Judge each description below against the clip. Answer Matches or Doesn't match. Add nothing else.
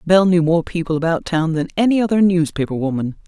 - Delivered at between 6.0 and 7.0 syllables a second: Matches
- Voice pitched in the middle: Matches